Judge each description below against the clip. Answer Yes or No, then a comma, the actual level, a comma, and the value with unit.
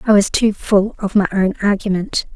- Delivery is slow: No, fast, 205 wpm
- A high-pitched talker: Yes, high, 200 Hz